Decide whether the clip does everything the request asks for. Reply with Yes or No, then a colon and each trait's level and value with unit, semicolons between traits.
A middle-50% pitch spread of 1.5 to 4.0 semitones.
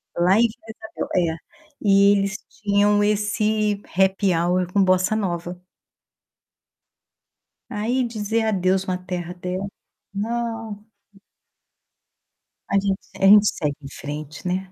Yes: narrow, 2.6 semitones